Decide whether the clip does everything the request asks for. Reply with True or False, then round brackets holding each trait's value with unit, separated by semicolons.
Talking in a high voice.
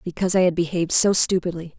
False (175 Hz)